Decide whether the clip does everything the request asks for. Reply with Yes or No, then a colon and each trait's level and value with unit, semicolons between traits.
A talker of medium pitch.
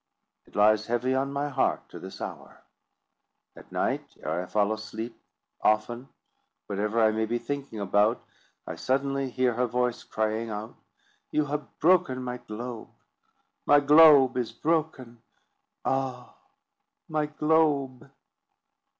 No: low, 125 Hz